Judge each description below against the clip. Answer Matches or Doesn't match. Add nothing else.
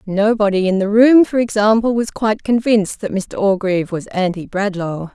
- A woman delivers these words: Matches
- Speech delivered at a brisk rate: Doesn't match